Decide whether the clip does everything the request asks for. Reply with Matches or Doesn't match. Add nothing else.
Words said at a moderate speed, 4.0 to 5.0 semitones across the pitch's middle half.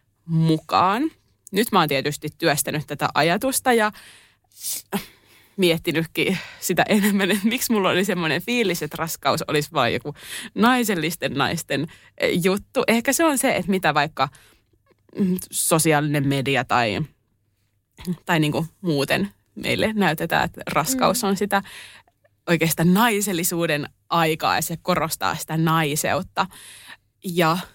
Matches